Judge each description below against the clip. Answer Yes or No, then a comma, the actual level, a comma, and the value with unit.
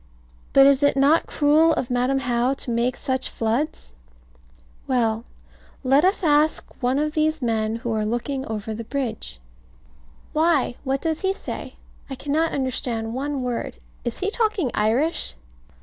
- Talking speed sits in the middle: Yes, average, 150 wpm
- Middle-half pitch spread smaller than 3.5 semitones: No, average, 4.2 semitones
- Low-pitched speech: No, very high, 265 Hz